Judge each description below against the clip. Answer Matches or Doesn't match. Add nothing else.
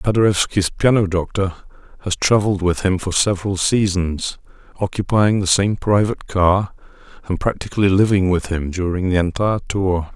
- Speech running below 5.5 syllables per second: Matches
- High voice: Doesn't match